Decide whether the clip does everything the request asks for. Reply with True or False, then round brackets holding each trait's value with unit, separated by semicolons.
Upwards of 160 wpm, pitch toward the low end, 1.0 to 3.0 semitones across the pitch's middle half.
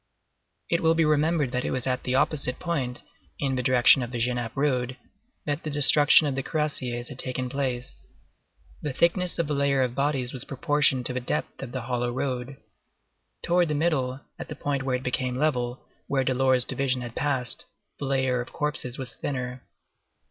True (190 wpm; 130 Hz; 2.6 semitones)